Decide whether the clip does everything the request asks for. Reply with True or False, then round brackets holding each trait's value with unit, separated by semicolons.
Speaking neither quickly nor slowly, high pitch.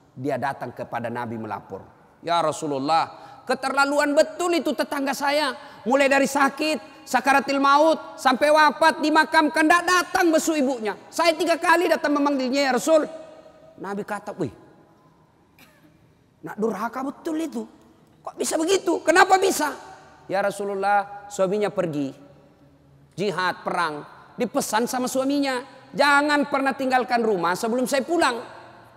True (125 wpm; 270 Hz)